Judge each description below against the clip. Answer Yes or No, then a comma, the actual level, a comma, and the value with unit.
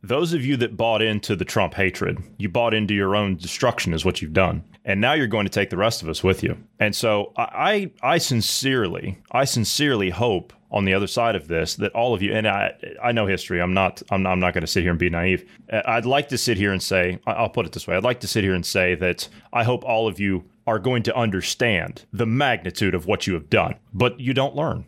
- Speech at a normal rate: No, fast, 260 wpm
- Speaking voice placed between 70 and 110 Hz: Yes, low, 105 Hz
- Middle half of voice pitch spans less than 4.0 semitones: No, average, 4.3 semitones